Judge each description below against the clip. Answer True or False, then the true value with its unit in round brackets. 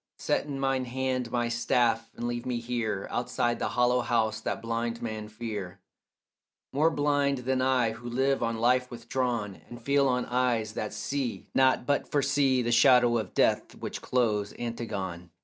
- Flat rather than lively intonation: True (2.3 semitones)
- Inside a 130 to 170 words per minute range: True (165 wpm)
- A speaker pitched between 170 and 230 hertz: False (120 Hz)